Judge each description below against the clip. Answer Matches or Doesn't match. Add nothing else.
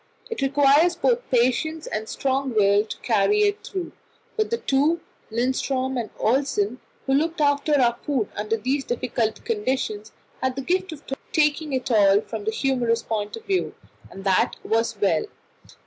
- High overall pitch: Matches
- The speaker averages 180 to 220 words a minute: Doesn't match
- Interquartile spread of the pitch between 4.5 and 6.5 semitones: Matches